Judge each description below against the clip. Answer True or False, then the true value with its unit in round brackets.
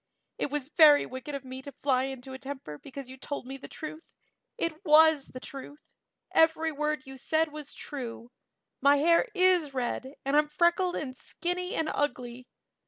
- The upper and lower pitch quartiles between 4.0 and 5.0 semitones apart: False (3.1 semitones)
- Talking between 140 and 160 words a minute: False (175 wpm)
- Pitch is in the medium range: False (285 Hz)